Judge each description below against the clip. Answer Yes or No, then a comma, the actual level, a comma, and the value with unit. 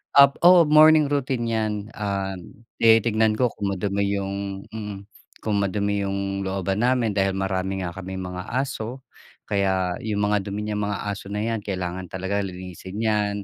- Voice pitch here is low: Yes, low, 100 Hz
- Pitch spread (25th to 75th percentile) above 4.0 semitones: No, narrow, 2.5 semitones